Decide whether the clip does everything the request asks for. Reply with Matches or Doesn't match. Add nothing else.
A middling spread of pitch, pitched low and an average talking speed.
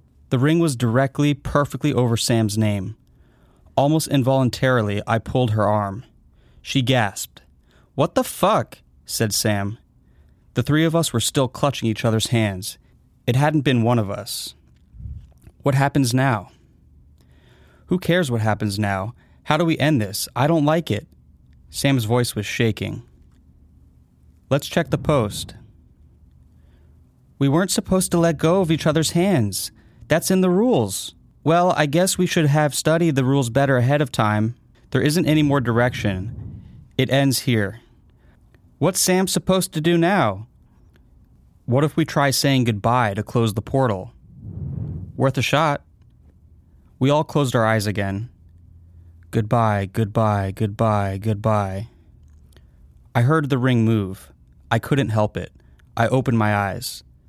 Doesn't match